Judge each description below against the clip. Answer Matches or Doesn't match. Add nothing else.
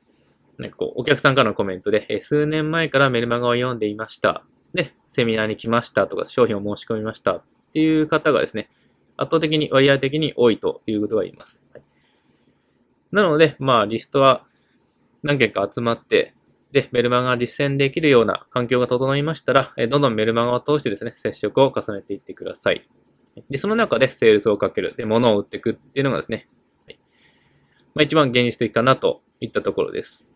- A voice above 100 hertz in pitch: Matches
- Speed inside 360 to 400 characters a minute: Matches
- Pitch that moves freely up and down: Doesn't match